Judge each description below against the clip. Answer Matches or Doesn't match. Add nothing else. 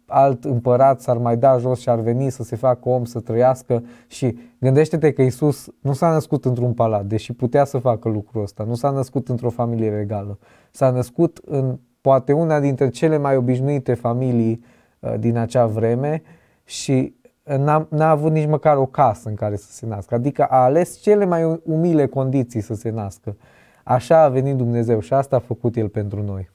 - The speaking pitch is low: Matches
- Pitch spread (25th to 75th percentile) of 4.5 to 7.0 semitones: Doesn't match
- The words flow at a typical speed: Doesn't match